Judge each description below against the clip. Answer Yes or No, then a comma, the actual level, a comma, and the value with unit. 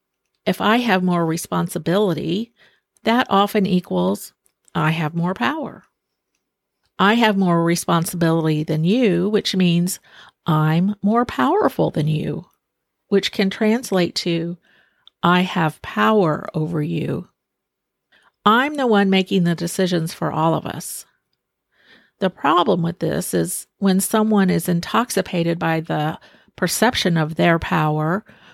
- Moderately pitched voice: Yes, medium, 180 Hz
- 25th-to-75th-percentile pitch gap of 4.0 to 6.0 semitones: No, average, 3.4 semitones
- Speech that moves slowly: Yes, slow, 125 wpm